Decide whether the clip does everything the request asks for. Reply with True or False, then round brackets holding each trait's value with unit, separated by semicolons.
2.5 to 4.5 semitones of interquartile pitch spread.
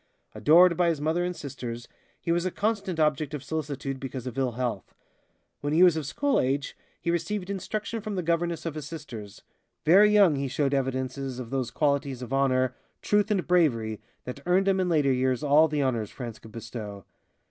False (5.1 semitones)